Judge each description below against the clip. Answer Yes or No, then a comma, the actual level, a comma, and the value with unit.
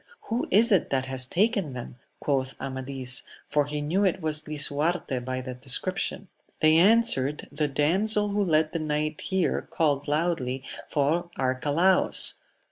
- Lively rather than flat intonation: No, average, 4.9 semitones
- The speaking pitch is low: No, medium, 150 Hz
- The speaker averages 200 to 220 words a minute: No, average, 145 wpm